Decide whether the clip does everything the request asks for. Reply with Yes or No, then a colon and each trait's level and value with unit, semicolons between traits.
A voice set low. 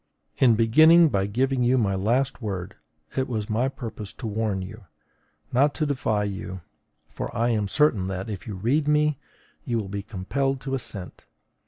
Yes: low, 115 Hz